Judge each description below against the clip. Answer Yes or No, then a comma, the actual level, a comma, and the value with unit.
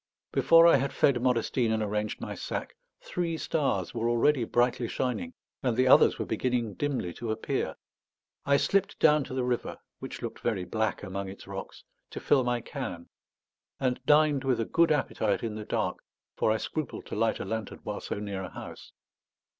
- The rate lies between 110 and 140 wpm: No, average, 185 wpm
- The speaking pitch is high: No, low, 120 Hz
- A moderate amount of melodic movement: Yes, average, 4.5 semitones